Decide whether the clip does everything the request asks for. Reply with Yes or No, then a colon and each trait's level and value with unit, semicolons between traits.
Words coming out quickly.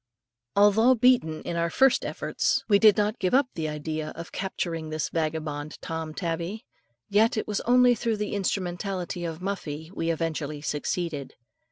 No: average, 160 wpm